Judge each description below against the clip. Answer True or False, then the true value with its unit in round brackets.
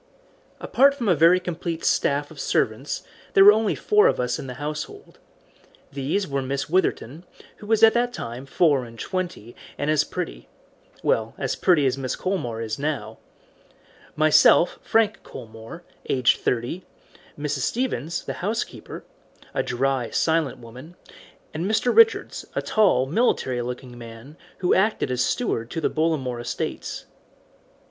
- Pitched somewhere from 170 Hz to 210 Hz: False (150 Hz)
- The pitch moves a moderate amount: False (6.7 semitones)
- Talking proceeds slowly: False (150 wpm)